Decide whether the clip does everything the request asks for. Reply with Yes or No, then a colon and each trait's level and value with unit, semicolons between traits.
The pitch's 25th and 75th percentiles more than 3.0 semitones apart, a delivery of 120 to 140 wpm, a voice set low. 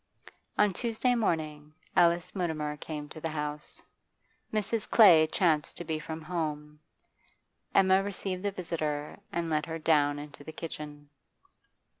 No: average, 3.4 semitones; slow, 135 wpm; medium, 160 Hz